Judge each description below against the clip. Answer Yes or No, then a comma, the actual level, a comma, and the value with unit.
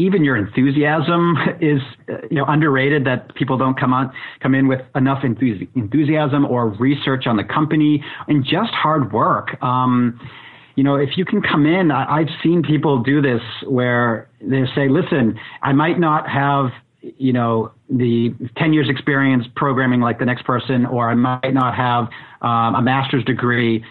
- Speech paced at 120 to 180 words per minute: Yes, average, 170 wpm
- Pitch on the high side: No, low, 135 Hz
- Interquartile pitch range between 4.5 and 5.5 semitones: No, average, 3.1 semitones